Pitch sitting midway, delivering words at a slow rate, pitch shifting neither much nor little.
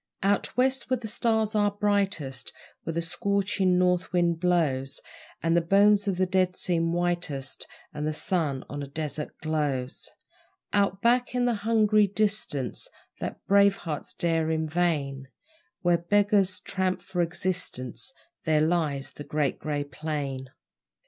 No: medium, 175 Hz; average, 145 wpm; average, 4.8 semitones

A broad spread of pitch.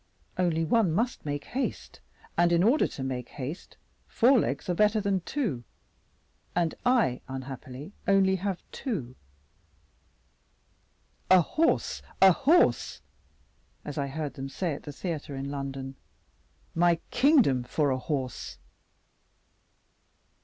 Yes: wide, 6.8 semitones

